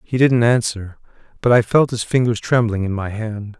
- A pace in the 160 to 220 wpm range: Yes, average, 200 wpm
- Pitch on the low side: Yes, low, 115 Hz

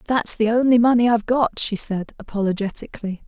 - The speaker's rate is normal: Yes, average, 165 wpm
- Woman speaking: Yes, female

